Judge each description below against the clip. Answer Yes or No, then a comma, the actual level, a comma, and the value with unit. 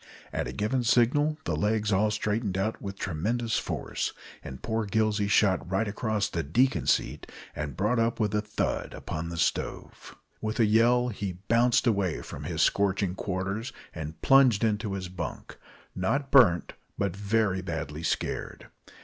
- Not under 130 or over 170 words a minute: Yes, average, 160 wpm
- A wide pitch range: No, average, 3.5 semitones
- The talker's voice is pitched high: No, low, 105 Hz